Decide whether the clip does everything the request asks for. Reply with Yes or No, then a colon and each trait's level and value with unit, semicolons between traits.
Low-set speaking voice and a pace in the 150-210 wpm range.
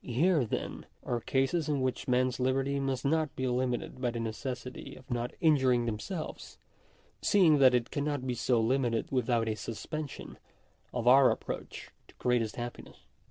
Yes: low, 130 Hz; average, 165 wpm